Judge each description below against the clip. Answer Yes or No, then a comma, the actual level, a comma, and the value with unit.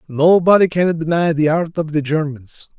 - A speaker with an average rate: Yes, average, 170 wpm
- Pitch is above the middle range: No, medium, 160 Hz